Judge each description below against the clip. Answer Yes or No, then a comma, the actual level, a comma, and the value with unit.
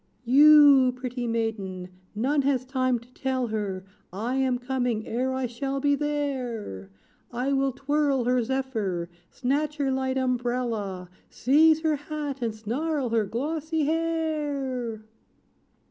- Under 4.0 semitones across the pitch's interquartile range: Yes, average, 3.6 semitones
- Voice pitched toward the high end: Yes, very high, 260 Hz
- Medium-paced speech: No, slow, 130 wpm